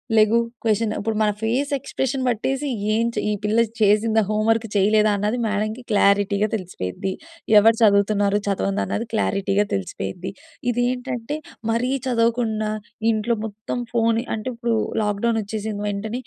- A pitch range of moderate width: No, narrow, 2.2 semitones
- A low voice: No, high, 215 Hz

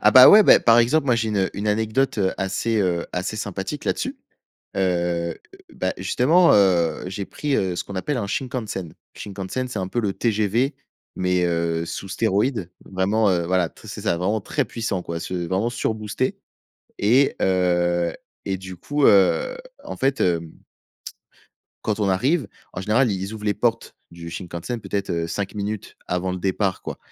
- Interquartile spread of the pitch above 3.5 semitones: Yes, average, 4.0 semitones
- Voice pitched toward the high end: No, low, 100 Hz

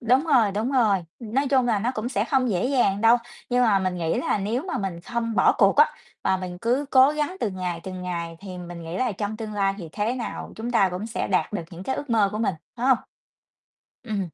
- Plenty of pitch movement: No, average, 4.7 semitones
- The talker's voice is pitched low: No, high, 215 Hz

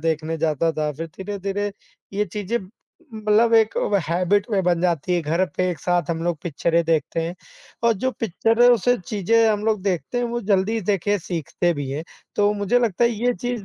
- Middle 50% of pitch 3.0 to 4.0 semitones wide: No, average, 4.6 semitones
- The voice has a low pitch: No, high, 195 Hz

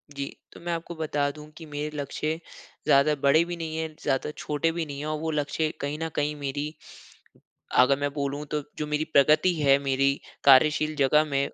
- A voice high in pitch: No, medium, 150 Hz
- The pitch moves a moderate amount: No, narrow, 1.8 semitones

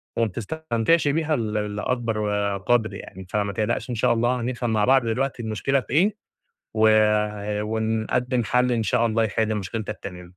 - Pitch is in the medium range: No, low, 115 Hz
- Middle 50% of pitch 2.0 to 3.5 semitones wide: Yes, average, 2.7 semitones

